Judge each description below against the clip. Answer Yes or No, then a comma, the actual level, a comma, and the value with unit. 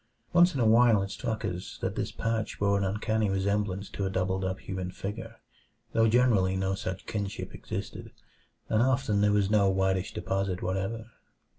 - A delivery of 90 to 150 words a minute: No, average, 175 wpm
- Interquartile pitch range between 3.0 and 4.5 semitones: No, narrow, 2.6 semitones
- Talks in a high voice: No, low, 100 Hz